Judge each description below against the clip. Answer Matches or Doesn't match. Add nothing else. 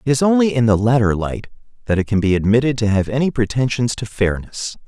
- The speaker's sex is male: Matches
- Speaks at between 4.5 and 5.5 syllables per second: Doesn't match